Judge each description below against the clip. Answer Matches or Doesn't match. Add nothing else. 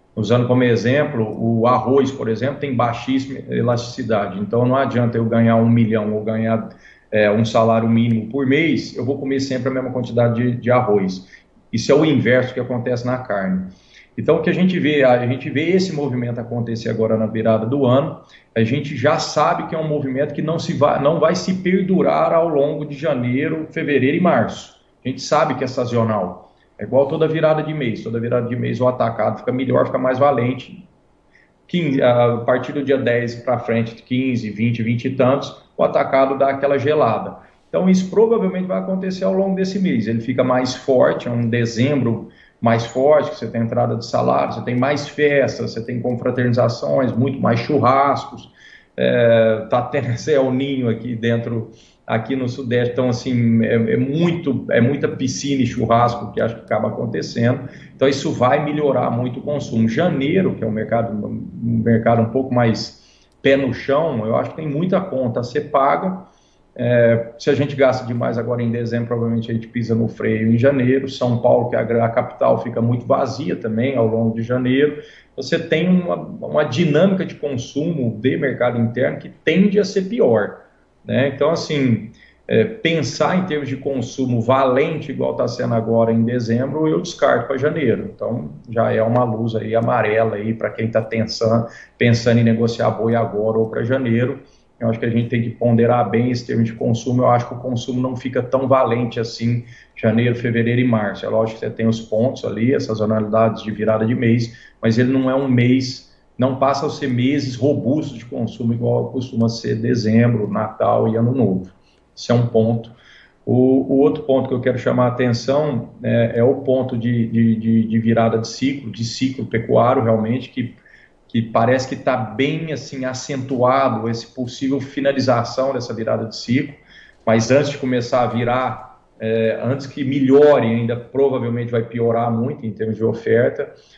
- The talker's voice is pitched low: Matches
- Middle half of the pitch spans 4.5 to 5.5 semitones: Doesn't match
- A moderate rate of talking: Doesn't match